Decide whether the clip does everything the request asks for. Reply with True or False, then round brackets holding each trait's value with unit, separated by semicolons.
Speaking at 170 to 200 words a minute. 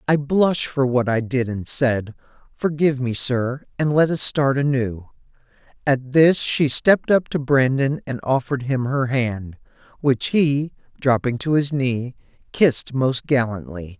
False (160 wpm)